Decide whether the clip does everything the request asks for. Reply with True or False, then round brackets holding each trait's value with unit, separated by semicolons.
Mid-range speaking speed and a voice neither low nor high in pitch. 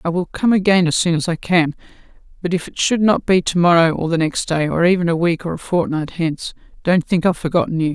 False (255 wpm; 170 Hz)